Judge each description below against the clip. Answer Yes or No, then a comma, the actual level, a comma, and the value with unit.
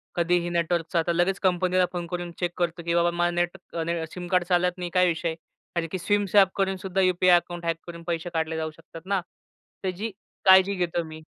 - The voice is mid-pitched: Yes, medium, 175 Hz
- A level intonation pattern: Yes, narrow, 1.4 semitones